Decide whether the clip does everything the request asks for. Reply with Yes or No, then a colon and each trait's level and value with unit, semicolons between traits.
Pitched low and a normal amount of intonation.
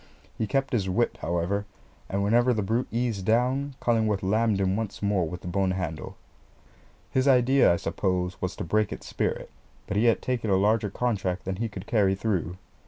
Yes: low, 105 Hz; average, 3.8 semitones